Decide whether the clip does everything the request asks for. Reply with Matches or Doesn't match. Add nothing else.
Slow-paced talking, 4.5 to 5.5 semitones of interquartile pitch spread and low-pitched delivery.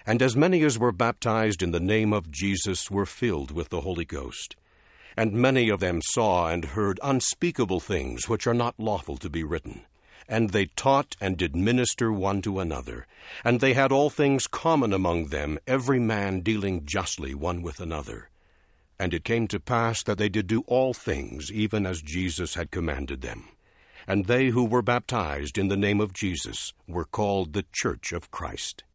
Doesn't match